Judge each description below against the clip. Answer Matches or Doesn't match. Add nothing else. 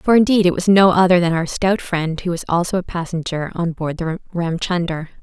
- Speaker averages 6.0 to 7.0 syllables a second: Doesn't match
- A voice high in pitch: Doesn't match